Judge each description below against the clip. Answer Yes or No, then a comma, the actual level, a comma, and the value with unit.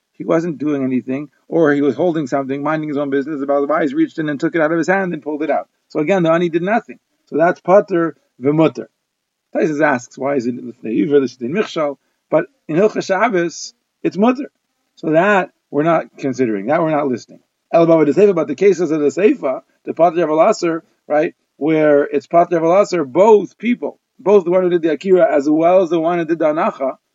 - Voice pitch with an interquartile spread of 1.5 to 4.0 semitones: No, average, 4.9 semitones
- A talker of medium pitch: Yes, medium, 165 Hz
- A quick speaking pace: Yes, fast, 215 wpm